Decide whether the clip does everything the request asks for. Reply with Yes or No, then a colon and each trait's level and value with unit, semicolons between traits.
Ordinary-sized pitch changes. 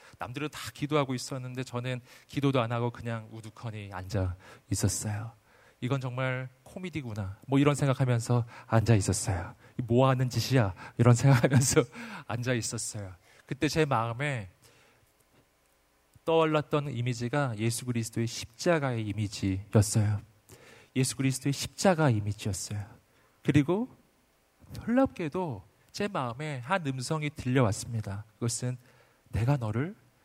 Yes: average, 3.9 semitones